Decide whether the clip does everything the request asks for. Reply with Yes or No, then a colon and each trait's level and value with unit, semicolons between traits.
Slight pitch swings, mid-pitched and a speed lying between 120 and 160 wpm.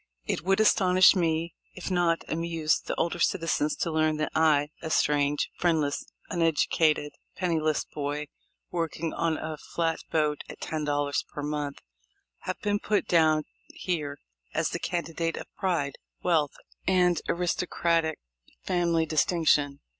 Yes: narrow, 2.3 semitones; medium, 160 Hz; slow, 135 wpm